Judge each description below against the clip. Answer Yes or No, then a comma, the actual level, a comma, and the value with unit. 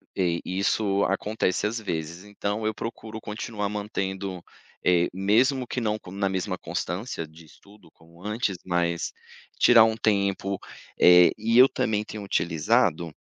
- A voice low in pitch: Yes, low, 100 Hz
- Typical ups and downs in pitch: Yes, average, 3.4 semitones